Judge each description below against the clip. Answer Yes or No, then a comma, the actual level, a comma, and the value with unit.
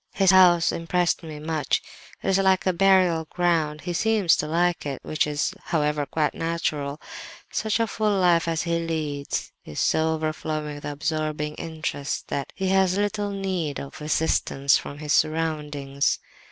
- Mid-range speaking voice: Yes, medium, 160 Hz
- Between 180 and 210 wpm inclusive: No, average, 160 wpm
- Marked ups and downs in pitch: No, average, 3.3 semitones